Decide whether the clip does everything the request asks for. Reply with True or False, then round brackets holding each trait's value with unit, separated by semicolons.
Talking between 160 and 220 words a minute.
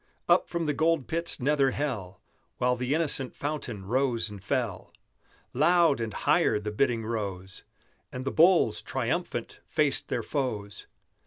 False (145 wpm)